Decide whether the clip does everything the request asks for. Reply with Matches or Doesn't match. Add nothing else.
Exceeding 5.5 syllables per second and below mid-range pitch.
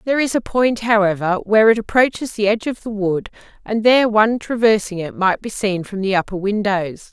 Doesn't match